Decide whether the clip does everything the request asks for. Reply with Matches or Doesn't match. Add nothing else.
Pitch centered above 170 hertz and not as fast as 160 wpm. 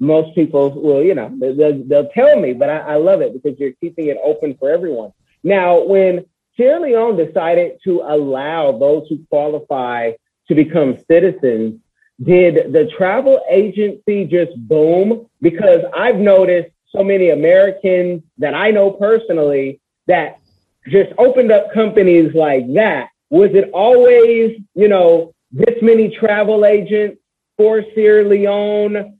Matches